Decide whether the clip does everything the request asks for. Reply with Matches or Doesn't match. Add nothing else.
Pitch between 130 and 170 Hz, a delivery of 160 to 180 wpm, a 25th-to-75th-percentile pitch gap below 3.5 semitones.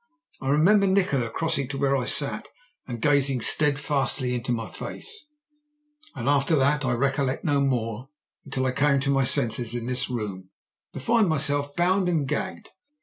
Matches